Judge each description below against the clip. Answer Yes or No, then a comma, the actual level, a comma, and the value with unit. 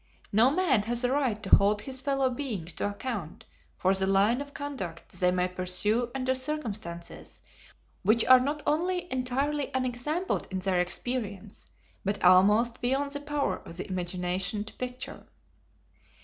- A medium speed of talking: Yes, average, 150 wpm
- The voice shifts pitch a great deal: Yes, wide, 6.1 semitones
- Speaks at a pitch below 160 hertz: No, high, 230 Hz